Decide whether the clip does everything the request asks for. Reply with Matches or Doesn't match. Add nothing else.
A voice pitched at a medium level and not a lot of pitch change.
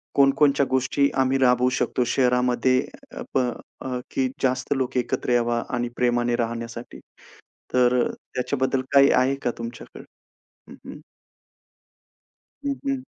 Doesn't match